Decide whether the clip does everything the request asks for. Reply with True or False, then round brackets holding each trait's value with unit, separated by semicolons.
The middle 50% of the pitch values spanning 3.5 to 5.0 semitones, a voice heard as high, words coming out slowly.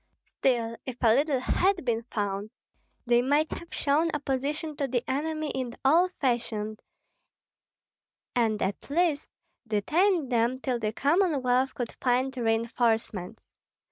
True (4.3 semitones; 255 Hz; 125 wpm)